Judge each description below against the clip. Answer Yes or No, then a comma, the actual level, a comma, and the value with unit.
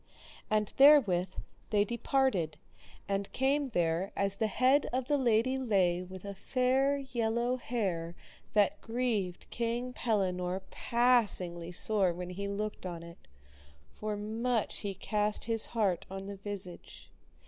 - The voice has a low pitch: No, high, 210 Hz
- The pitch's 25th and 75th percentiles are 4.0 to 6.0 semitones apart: Yes, average, 4.7 semitones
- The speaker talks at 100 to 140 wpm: Yes, slow, 135 wpm